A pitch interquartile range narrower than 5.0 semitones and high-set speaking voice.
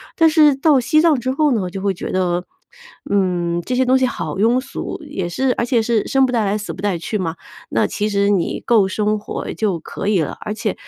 No: wide, 5.4 semitones; high, 210 Hz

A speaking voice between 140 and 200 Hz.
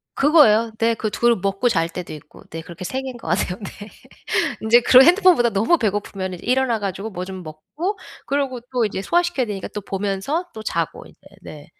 No: high, 220 Hz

